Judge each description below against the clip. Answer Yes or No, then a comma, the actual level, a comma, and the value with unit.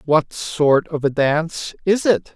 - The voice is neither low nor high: Yes, medium, 160 Hz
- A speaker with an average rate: Yes, average, 180 wpm